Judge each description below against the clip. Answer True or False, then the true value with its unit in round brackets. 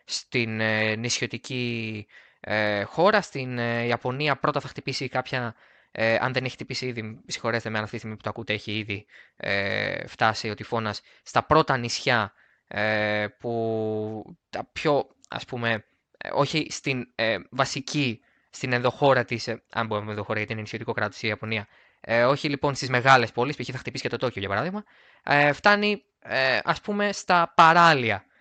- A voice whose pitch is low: True (120 Hz)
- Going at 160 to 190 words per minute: True (170 wpm)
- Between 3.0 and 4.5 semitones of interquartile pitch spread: True (3.9 semitones)